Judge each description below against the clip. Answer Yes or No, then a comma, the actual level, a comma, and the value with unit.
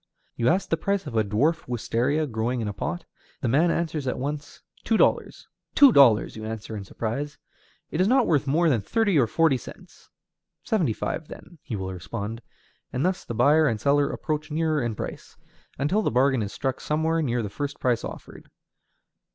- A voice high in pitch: No, medium, 140 Hz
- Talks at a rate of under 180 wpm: No, average, 190 wpm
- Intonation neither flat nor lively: No, wide, 5.7 semitones